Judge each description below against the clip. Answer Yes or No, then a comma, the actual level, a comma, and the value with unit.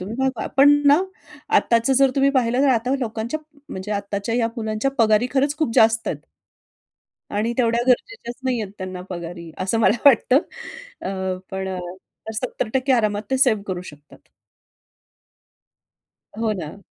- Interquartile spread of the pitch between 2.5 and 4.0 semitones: No, average, 4.6 semitones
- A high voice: Yes, high, 225 Hz